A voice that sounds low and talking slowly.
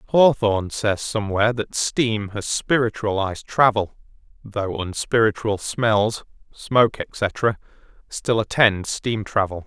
Yes: low, 110 Hz; slow, 105 wpm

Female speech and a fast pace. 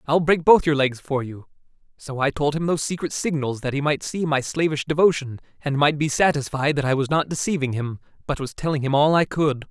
No: male; fast, 235 wpm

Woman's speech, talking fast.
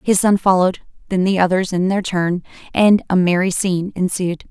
No: female; average, 185 wpm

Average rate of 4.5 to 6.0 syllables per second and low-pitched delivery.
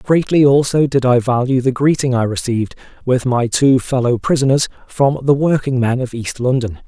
Yes: 5.1 syllables/s; low, 130 Hz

